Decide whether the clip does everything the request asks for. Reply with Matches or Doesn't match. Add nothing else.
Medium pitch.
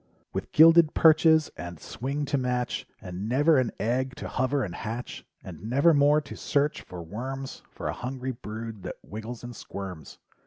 Doesn't match